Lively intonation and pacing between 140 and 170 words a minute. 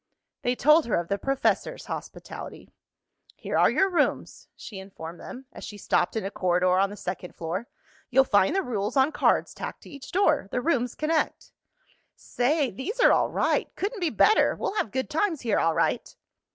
No: wide, 7.9 semitones; average, 190 wpm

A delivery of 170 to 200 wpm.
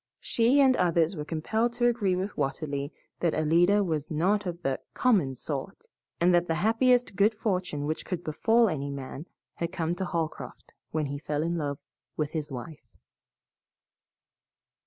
No: average, 160 wpm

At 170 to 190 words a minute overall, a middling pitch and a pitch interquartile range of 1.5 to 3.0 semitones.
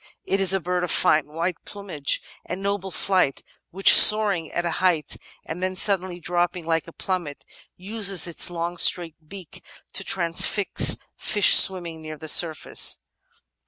No: average, 155 wpm; medium, 175 Hz; average, 2.7 semitones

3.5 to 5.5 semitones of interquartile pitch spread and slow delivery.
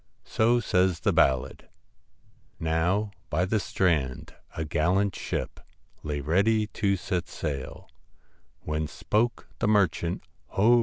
Yes: average, 5.0 semitones; slow, 120 wpm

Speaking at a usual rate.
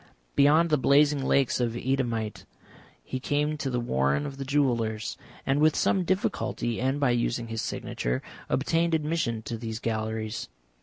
Yes: average, 155 wpm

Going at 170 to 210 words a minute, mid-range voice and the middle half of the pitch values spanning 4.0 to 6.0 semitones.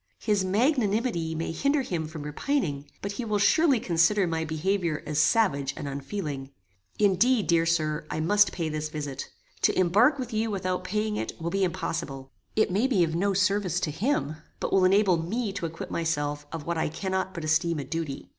Yes: average, 195 wpm; medium, 175 Hz; average, 4.8 semitones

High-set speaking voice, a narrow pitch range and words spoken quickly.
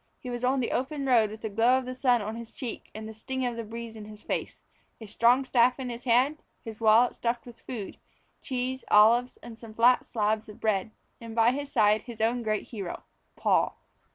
Yes: high, 235 Hz; narrow, 2.3 semitones; fast, 225 wpm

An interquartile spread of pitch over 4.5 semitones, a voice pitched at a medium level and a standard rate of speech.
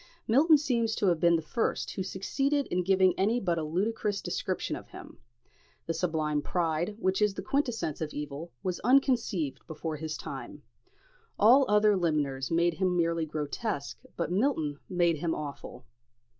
Yes: average, 5.2 semitones; medium, 175 Hz; average, 160 wpm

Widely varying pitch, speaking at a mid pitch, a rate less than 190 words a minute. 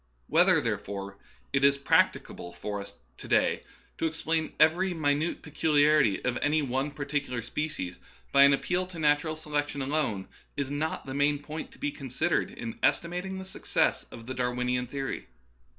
No: average, 3.7 semitones; medium, 145 Hz; average, 165 wpm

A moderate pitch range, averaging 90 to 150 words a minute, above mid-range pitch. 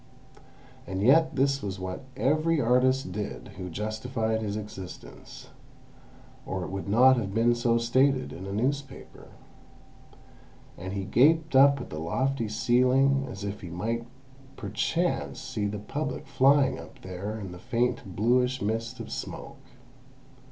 No: average, 4.9 semitones; average, 140 wpm; low, 115 Hz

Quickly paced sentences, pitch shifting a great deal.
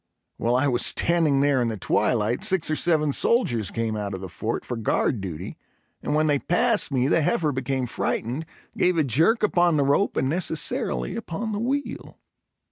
No: average, 190 wpm; wide, 6.4 semitones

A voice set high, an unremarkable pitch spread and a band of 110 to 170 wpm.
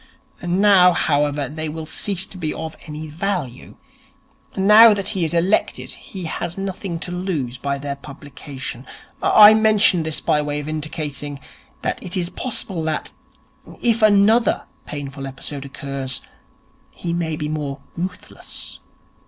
No: medium, 160 Hz; average, 4.8 semitones; average, 140 wpm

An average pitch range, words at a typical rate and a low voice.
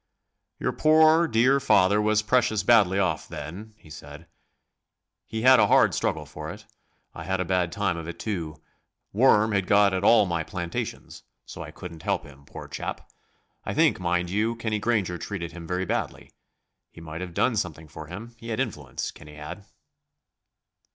Yes: average, 4.6 semitones; average, 180 wpm; very low, 95 Hz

